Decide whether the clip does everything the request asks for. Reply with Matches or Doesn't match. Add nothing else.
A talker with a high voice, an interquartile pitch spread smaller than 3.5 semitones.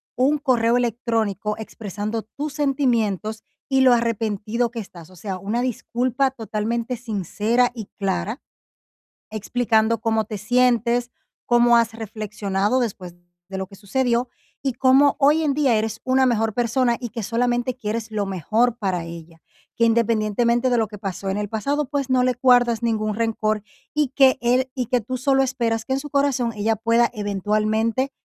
Matches